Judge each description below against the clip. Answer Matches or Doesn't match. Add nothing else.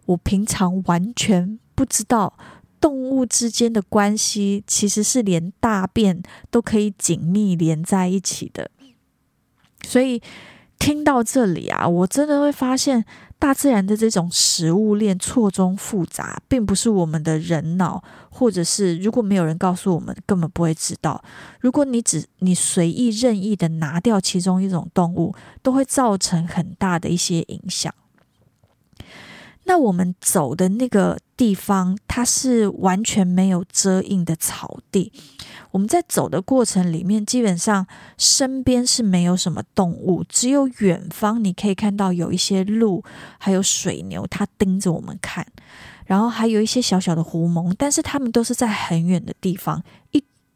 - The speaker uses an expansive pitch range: Doesn't match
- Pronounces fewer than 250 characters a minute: Matches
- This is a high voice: Matches